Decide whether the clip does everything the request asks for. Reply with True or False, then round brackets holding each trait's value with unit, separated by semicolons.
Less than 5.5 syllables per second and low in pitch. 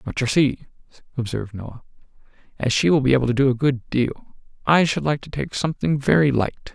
False (5.6 syllables/s; 130 Hz)